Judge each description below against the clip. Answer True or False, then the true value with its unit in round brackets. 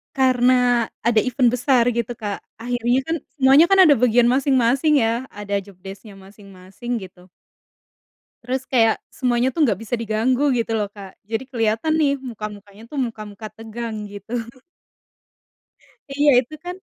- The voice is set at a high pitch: True (235 Hz)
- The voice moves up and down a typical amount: True (3.5 semitones)